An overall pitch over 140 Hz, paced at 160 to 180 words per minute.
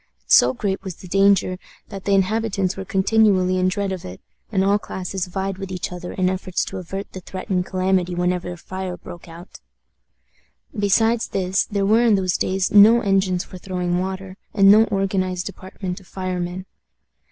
Yes: high, 190 Hz; average, 175 wpm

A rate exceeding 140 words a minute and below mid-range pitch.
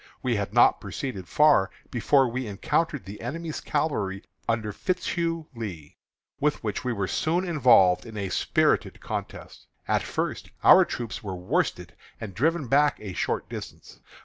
Yes: average, 150 wpm; low, 120 Hz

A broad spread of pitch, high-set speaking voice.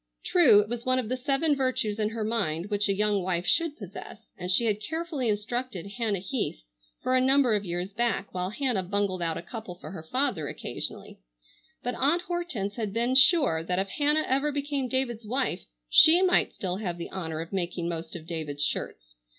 Yes: wide, 6.2 semitones; high, 215 Hz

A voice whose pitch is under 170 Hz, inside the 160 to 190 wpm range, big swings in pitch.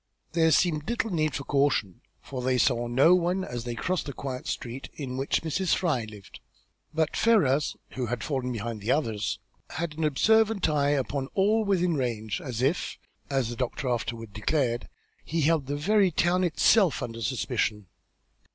Yes: medium, 140 Hz; average, 180 wpm; wide, 5.8 semitones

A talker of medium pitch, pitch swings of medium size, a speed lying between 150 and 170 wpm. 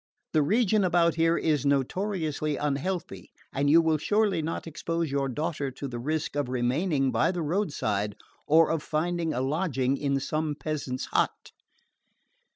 Yes: medium, 155 Hz; average, 3.5 semitones; average, 155 wpm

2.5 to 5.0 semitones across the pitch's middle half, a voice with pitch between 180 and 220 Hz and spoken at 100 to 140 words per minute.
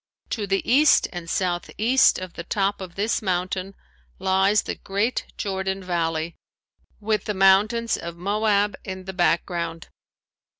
Yes: average, 2.8 semitones; high, 190 Hz; slow, 135 wpm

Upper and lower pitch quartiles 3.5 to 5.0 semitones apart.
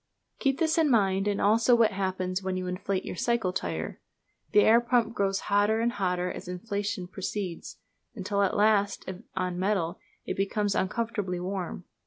No: average, 3.0 semitones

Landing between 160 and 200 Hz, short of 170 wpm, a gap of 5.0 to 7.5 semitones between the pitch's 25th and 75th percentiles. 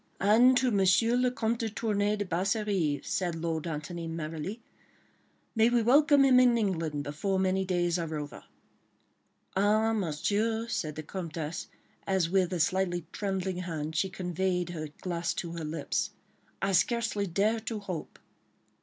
No: high, 190 Hz; average, 150 wpm; average, 4.6 semitones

